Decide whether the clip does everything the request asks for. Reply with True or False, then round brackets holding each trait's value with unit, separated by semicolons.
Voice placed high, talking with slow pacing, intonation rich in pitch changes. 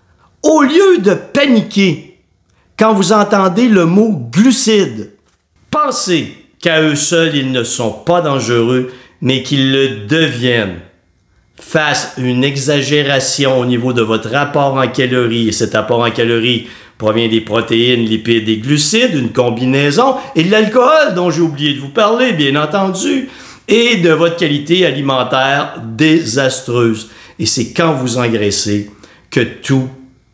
False (140 Hz; 140 wpm; 6.7 semitones)